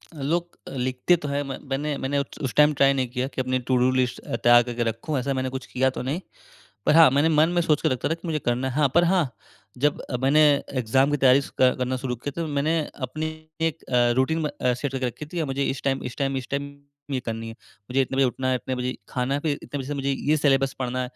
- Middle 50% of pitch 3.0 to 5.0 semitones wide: No, narrow, 2.5 semitones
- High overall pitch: No, low, 135 Hz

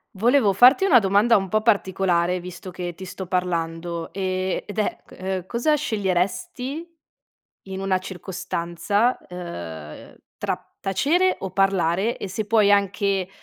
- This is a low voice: No, high, 190 Hz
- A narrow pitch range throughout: No, average, 3.1 semitones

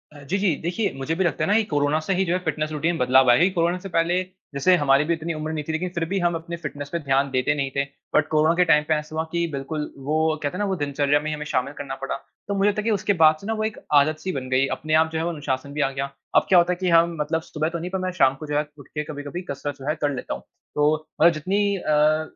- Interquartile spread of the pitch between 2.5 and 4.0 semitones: Yes, average, 3.2 semitones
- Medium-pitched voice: Yes, medium, 155 Hz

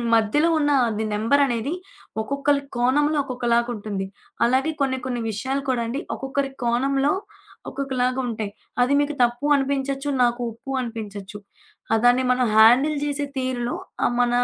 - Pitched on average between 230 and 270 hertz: Yes, very high, 255 Hz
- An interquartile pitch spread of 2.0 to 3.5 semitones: Yes, average, 2.8 semitones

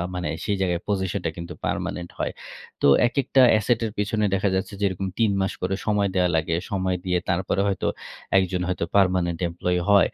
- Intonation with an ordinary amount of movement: No, narrow, 2.3 semitones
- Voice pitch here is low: Yes, very low, 95 Hz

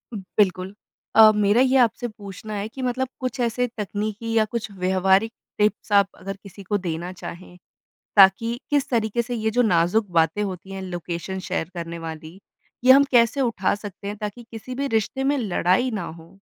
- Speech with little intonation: No, average, 3.9 semitones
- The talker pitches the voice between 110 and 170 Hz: No, high, 205 Hz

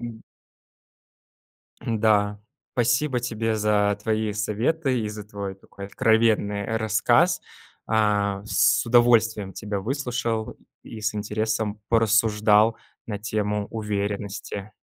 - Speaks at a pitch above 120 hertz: No, low, 110 Hz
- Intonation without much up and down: Yes, narrow, 1.6 semitones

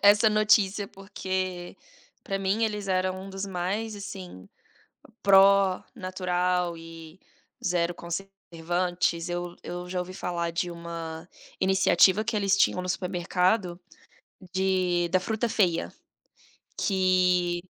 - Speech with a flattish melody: Yes, narrow, 1.8 semitones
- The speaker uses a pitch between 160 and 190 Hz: Yes, medium, 185 Hz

